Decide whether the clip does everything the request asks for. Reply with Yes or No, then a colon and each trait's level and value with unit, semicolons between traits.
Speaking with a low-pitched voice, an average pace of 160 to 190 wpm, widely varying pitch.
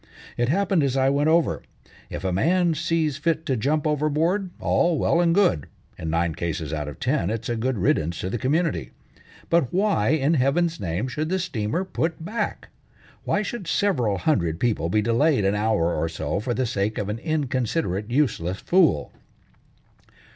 Yes: low, 130 Hz; average, 175 wpm; wide, 8.6 semitones